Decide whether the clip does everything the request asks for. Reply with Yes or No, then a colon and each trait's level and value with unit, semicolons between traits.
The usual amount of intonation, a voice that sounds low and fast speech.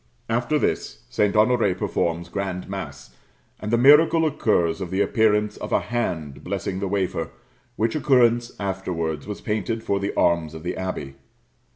No: average, 4.8 semitones; low, 100 Hz; average, 160 wpm